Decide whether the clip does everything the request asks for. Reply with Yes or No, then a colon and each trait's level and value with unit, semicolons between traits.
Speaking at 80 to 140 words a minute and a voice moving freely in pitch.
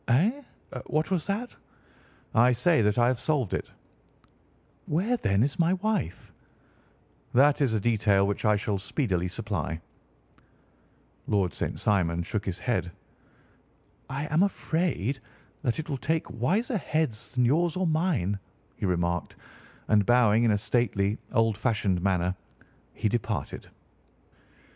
Yes: slow, 135 wpm; wide, 7.6 semitones